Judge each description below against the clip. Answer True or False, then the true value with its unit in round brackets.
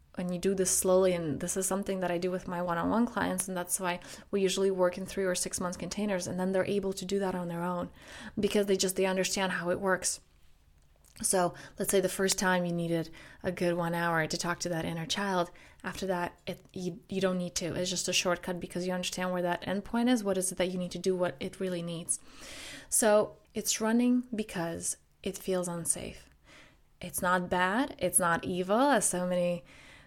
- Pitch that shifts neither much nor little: False (1.6 semitones)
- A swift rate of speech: True (225 wpm)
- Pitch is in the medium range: True (180 Hz)